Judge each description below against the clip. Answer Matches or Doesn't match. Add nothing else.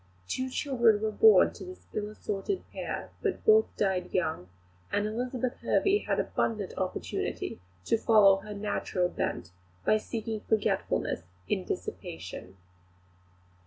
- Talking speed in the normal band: Doesn't match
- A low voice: Doesn't match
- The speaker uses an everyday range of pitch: Matches